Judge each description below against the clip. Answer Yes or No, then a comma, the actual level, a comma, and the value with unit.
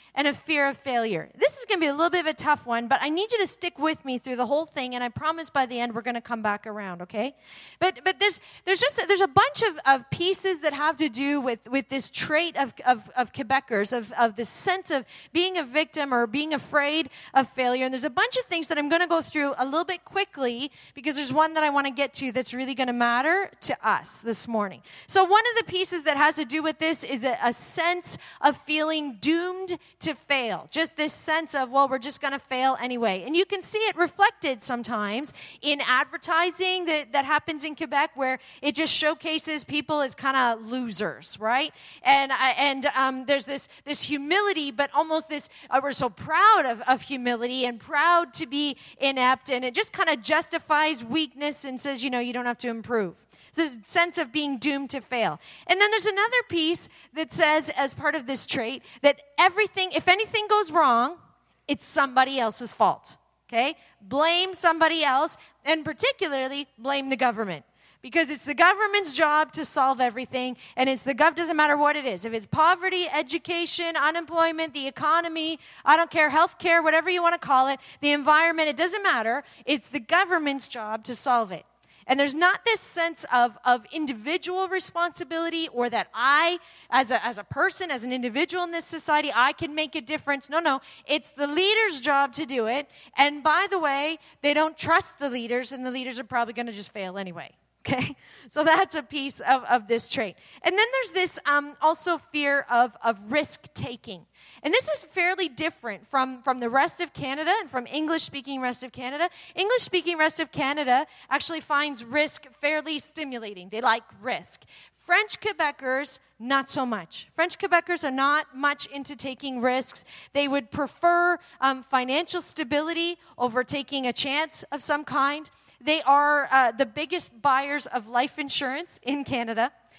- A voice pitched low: No, very high, 290 Hz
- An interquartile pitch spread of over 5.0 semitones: No, average, 4.2 semitones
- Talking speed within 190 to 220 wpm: Yes, average, 200 wpm